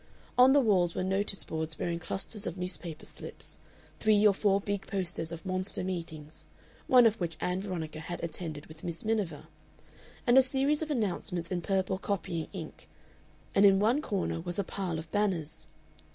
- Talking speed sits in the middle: Yes, average, 175 wpm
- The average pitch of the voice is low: No, medium, 185 Hz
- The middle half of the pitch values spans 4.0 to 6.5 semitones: No, average, 3.6 semitones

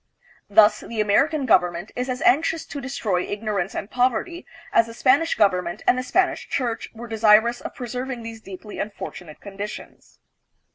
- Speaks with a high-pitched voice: Yes, high, 225 Hz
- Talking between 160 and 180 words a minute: Yes, average, 170 wpm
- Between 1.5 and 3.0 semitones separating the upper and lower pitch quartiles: No, average, 3.9 semitones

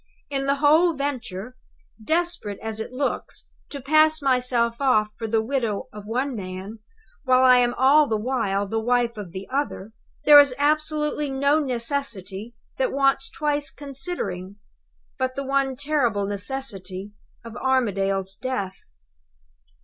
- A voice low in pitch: No, very high, 255 Hz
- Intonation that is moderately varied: Yes, average, 4.9 semitones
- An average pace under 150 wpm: Yes, average, 140 wpm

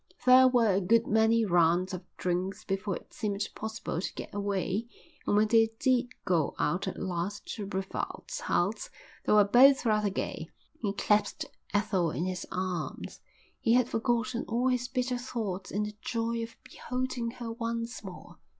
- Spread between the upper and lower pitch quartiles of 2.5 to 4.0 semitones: Yes, average, 3.7 semitones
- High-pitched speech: Yes, high, 215 Hz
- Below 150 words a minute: No, average, 170 wpm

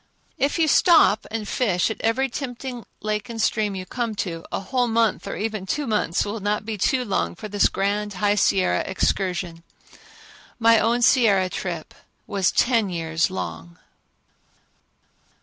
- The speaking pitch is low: No, high, 210 Hz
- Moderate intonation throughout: Yes, average, 3.6 semitones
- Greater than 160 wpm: No, average, 155 wpm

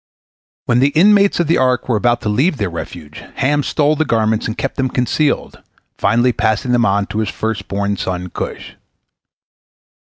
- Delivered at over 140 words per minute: Yes, average, 175 wpm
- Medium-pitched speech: No, low, 120 Hz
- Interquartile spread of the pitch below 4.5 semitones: No, average, 5.3 semitones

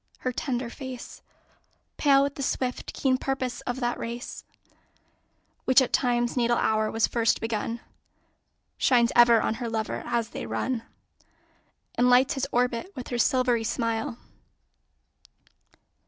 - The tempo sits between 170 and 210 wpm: No, slow, 135 wpm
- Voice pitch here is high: Yes, high, 245 Hz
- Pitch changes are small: Yes, narrow, 1.8 semitones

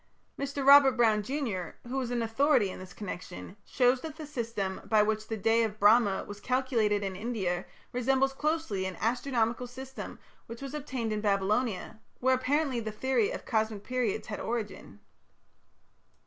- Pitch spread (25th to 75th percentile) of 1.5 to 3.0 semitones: No, average, 4.1 semitones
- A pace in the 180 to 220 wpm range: No, average, 160 wpm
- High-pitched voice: Yes, high, 230 Hz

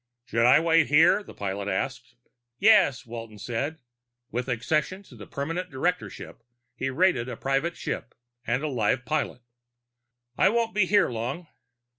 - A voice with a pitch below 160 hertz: Yes, low, 135 Hz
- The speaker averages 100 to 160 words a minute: Yes, average, 150 wpm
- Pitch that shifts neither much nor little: No, wide, 6.3 semitones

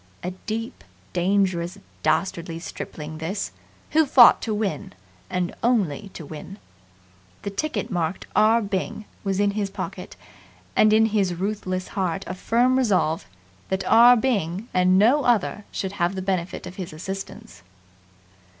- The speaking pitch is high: Yes, high, 195 Hz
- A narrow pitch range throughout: No, average, 3.2 semitones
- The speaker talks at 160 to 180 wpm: No, average, 140 wpm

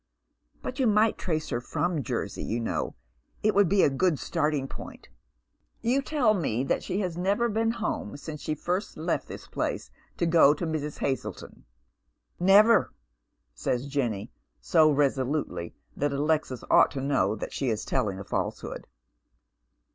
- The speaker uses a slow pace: No, average, 155 wpm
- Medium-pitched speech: Yes, medium, 155 Hz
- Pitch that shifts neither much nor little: No, wide, 6.4 semitones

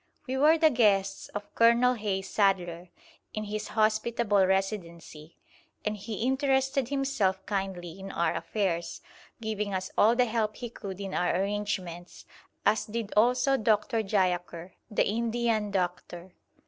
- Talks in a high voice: Yes, high, 210 Hz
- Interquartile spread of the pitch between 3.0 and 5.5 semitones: Yes, average, 3.4 semitones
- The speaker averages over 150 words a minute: No, slow, 135 wpm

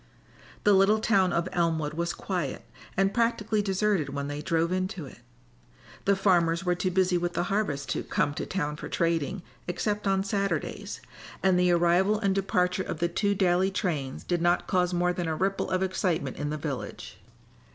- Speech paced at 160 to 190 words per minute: Yes, average, 185 wpm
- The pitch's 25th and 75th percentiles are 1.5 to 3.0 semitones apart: Yes, narrow, 2.6 semitones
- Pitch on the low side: No, medium, 180 Hz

